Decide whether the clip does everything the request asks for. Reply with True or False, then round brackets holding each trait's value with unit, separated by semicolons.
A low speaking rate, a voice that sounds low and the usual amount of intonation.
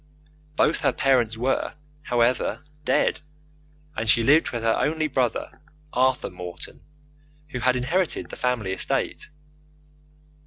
True (120 wpm; 125 Hz; 3.0 semitones)